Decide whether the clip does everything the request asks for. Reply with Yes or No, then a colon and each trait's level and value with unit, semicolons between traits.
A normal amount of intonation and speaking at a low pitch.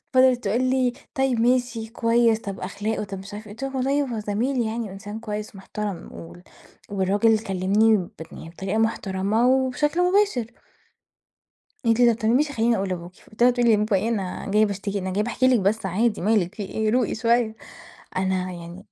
No: average, 3.5 semitones; high, 220 Hz